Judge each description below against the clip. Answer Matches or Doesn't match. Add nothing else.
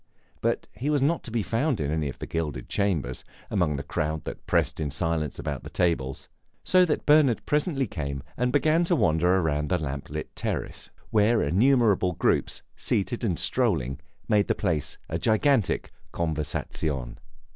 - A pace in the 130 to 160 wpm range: Doesn't match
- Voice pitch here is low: Matches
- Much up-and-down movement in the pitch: Matches